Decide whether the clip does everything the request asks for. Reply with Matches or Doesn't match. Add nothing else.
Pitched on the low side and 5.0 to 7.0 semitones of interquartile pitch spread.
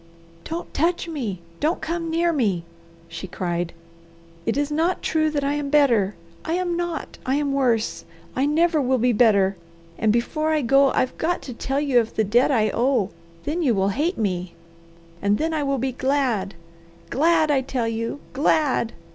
Doesn't match